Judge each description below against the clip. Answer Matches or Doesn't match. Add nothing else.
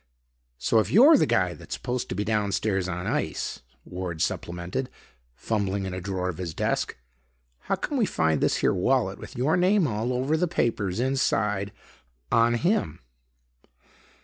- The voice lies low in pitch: Matches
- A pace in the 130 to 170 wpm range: Matches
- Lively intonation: Matches